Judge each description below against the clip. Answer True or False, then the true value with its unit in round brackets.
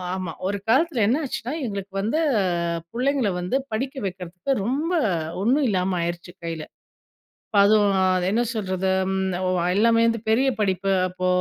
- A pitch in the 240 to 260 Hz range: False (205 Hz)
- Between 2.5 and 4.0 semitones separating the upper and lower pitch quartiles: False (4.8 semitones)